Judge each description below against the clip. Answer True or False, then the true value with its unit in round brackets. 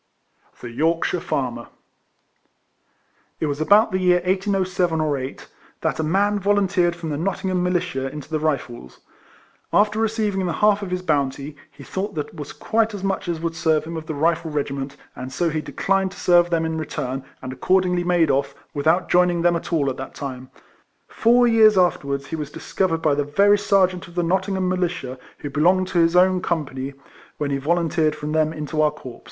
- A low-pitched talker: False (170 Hz)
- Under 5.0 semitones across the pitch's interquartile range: True (4.1 semitones)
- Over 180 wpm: True (190 wpm)